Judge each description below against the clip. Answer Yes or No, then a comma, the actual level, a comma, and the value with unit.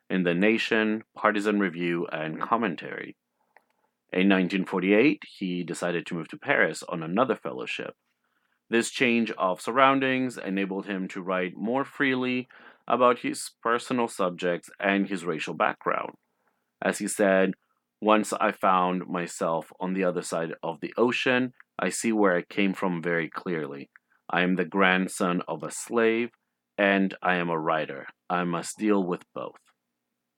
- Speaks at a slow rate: No, average, 150 wpm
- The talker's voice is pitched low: Yes, very low, 95 Hz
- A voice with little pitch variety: No, average, 3.7 semitones